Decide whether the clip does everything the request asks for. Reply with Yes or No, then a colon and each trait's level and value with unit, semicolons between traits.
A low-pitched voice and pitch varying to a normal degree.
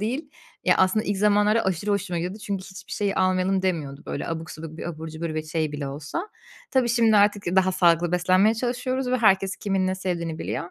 No: high, 190 Hz; average, 3.7 semitones